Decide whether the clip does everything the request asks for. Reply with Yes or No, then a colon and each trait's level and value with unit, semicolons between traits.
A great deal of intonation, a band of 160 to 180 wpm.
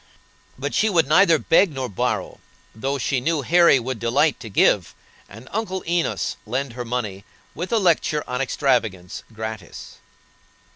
No: wide, 6.5 semitones; average, 150 wpm